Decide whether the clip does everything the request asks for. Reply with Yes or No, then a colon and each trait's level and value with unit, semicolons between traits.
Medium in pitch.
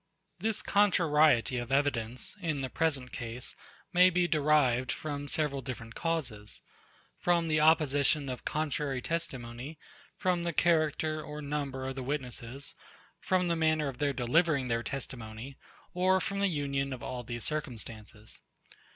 Yes: medium, 145 Hz